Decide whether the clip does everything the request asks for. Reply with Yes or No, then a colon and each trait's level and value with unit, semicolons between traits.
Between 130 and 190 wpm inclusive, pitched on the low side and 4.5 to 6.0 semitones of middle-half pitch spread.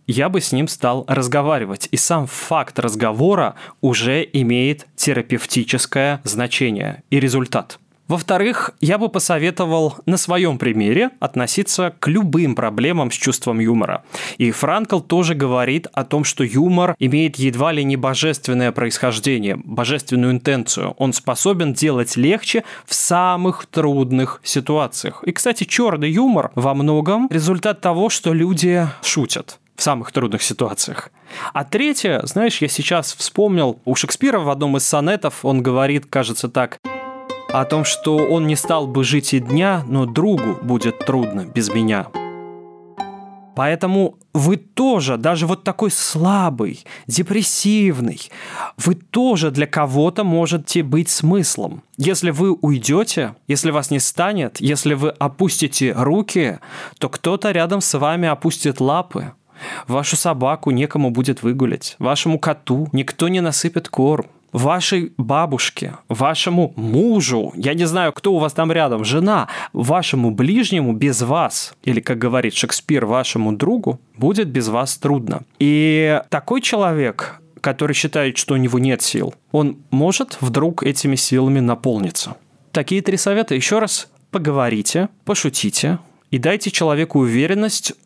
No: average, 135 wpm; medium, 150 Hz; average, 5.2 semitones